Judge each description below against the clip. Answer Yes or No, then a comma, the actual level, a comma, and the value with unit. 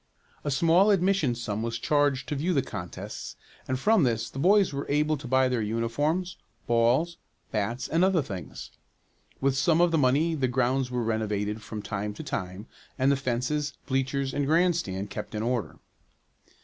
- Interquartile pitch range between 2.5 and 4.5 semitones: No, average, 5.0 semitones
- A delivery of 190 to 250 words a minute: No, average, 175 wpm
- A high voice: No, low, 130 Hz